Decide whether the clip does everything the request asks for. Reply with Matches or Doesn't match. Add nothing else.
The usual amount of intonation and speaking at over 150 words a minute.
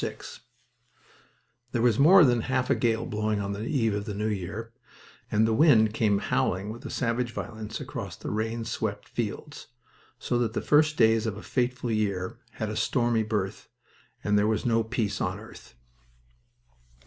Doesn't match